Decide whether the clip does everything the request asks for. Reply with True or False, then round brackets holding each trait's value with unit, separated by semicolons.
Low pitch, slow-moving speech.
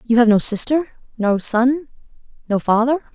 False (245 Hz; 115 wpm)